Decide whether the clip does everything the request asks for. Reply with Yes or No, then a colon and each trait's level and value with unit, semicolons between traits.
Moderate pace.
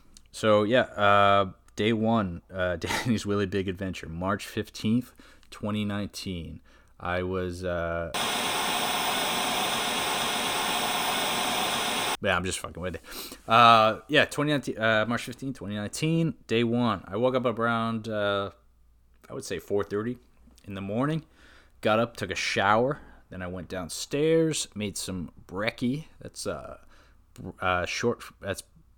No: slow, 125 wpm